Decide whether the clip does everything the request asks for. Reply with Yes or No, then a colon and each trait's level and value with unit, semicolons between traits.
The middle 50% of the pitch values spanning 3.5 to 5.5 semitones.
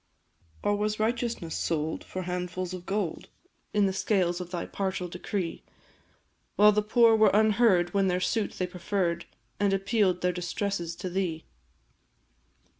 No: average, 2.8 semitones